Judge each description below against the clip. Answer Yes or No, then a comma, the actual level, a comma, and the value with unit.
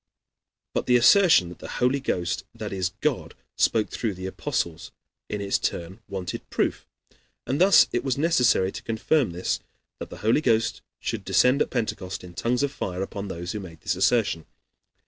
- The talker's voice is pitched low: Yes, low, 105 Hz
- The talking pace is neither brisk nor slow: Yes, average, 180 wpm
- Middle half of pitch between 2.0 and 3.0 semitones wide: No, average, 5.3 semitones